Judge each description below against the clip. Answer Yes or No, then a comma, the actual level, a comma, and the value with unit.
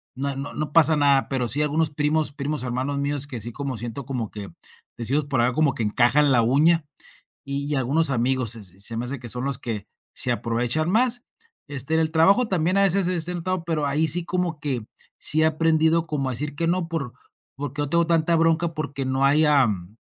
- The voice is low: No, medium, 145 Hz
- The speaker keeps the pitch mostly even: No, average, 4.0 semitones